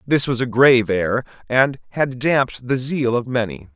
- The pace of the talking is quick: No, average, 190 wpm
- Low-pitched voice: Yes, low, 125 Hz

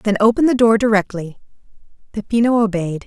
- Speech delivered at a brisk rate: No, slow, 135 wpm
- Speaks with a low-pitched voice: No, high, 210 Hz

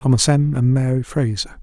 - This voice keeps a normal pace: Yes, average, 185 wpm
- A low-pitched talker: Yes, low, 130 Hz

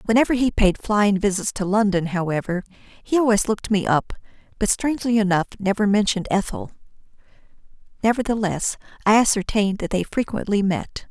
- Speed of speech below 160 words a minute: Yes, average, 140 wpm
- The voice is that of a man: No, female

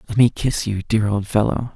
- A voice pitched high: No, low, 110 Hz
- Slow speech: No, fast, 240 wpm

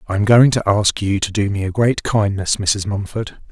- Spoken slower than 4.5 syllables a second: No, 5.0 syllables/s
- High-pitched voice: No, low, 105 Hz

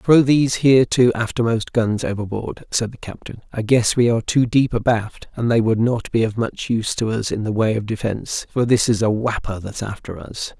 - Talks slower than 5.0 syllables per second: No, 5.3 syllables/s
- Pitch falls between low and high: No, low, 115 Hz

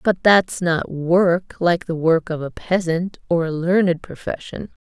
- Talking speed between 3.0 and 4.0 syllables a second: Yes, 3.9 syllables/s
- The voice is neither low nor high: Yes, medium, 175 Hz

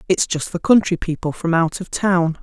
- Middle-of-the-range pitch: Yes, medium, 175 Hz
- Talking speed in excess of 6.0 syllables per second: No, 4.9 syllables/s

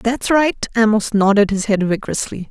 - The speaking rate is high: No, average, 165 wpm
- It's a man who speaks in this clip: No, female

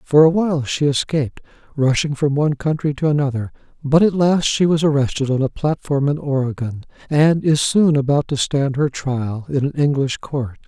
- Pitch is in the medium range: Yes, medium, 145 Hz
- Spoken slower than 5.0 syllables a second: No, 5.1 syllables/s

